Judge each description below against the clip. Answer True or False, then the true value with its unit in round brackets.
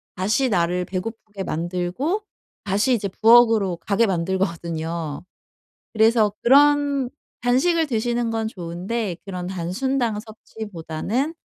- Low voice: False (210 Hz)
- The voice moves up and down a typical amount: True (5.0 semitones)